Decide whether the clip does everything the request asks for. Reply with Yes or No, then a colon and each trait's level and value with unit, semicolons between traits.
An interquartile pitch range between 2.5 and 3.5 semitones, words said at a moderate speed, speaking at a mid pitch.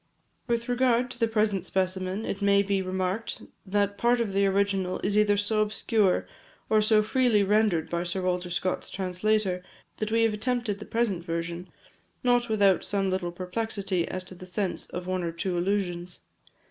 No: average, 2.9 semitones; average, 175 wpm; high, 200 Hz